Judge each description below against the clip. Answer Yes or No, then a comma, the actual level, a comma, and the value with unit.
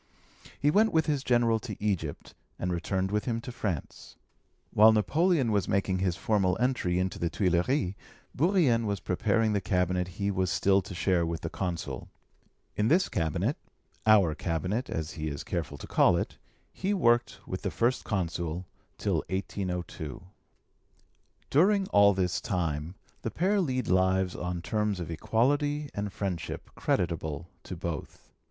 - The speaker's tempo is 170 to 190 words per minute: No, average, 155 wpm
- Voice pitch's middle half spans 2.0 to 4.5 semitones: No, average, 5.1 semitones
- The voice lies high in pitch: No, very low, 95 Hz